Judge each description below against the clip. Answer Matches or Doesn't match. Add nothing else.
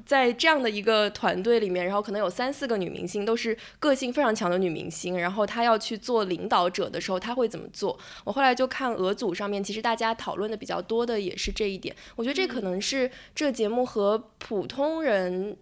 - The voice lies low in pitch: Doesn't match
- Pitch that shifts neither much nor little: Matches